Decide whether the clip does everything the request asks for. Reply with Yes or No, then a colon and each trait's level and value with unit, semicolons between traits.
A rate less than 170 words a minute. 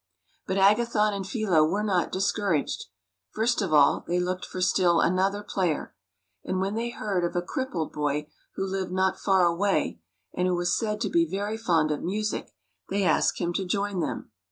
No: average, 185 wpm